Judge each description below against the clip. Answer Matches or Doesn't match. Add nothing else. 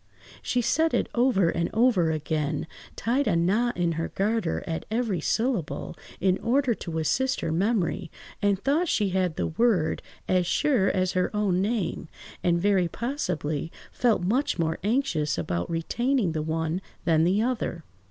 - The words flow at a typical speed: Matches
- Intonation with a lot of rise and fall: Matches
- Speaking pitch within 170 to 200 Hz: Matches